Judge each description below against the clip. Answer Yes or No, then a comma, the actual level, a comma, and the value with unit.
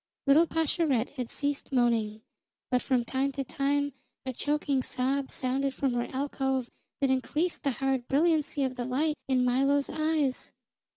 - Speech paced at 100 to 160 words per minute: Yes, average, 155 wpm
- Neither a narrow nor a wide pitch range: No, narrow, 2.1 semitones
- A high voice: Yes, very high, 270 Hz